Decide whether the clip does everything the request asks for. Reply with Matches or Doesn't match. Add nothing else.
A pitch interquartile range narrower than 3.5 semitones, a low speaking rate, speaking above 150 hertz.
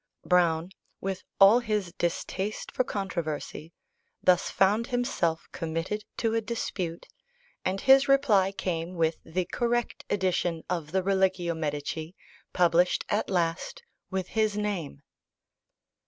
Doesn't match